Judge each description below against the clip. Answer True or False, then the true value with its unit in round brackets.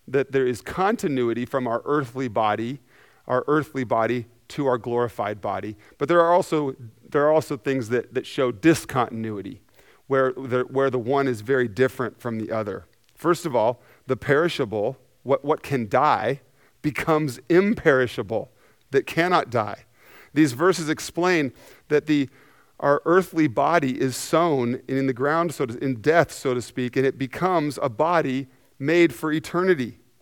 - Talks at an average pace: True (160 wpm)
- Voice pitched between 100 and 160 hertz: True (135 Hz)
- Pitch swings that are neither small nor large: True (3.6 semitones)